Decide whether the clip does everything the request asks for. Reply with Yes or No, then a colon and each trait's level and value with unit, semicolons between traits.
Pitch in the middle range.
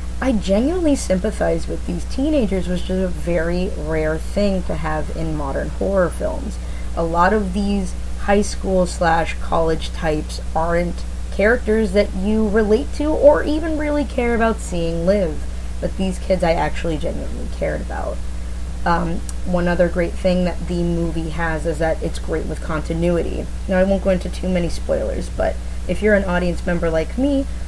Yes: medium, 180 Hz